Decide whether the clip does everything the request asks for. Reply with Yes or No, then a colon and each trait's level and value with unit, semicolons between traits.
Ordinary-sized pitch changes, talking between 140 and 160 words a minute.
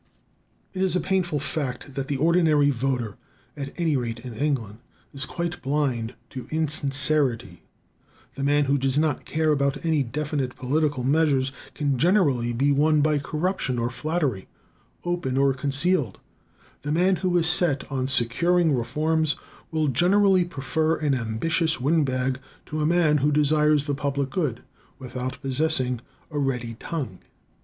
Yes: average, 3.5 semitones; average, 150 wpm